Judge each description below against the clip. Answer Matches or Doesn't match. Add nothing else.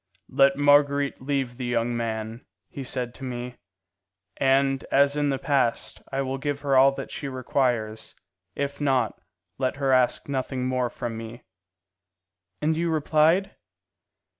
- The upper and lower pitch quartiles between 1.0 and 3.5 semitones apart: Matches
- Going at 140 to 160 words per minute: Matches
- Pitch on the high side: Doesn't match